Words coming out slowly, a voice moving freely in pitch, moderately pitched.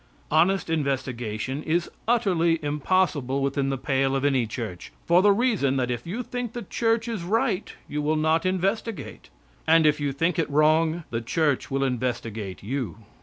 No: average, 170 wpm; wide, 5.7 semitones; medium, 155 Hz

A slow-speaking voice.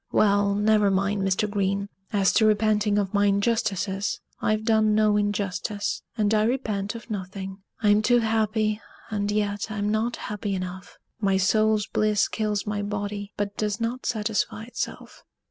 No: average, 155 wpm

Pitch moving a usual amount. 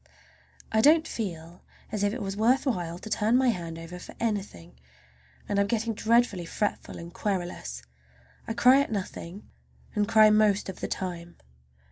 Yes: average, 4.3 semitones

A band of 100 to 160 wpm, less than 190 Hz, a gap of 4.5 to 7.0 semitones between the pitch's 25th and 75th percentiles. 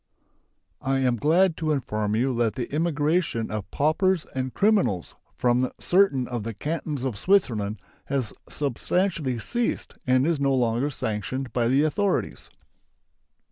Yes: average, 140 wpm; low, 135 Hz; average, 5.1 semitones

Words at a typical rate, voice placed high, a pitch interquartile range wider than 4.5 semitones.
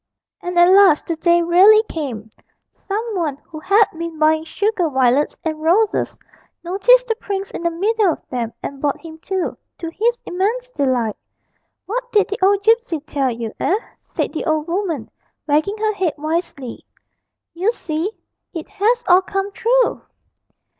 Yes: average, 160 wpm; very high, 350 Hz; average, 5.1 semitones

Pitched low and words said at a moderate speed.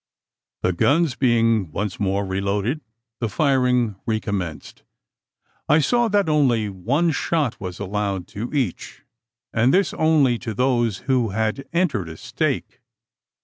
No: low, 115 Hz; slow, 130 wpm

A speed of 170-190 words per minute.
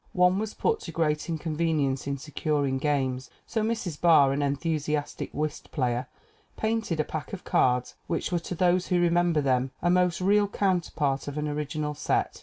Yes: average, 175 wpm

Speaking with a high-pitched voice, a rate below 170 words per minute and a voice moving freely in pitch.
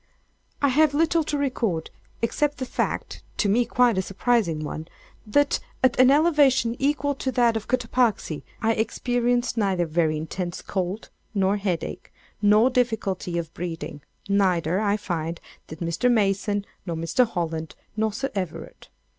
Yes: high, 210 Hz; average, 150 wpm; wide, 6.0 semitones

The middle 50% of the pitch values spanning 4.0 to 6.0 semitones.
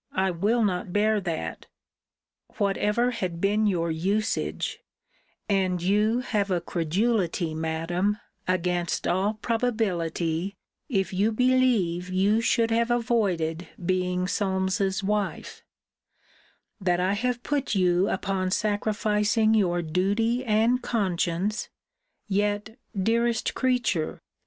No: average, 3.6 semitones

